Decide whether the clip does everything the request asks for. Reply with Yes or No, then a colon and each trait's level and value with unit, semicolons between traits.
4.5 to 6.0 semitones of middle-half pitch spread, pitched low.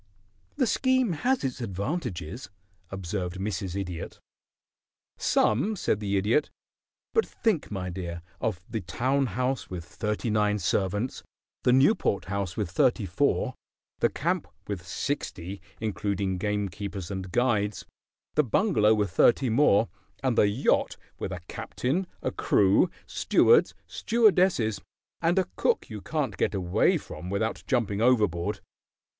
Yes: wide, 5.6 semitones; low, 105 Hz